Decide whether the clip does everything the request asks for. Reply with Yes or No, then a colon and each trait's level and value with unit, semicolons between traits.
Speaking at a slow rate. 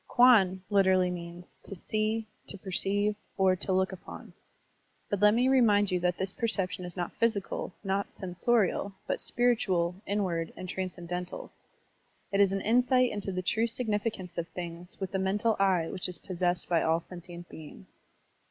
No: average, 170 wpm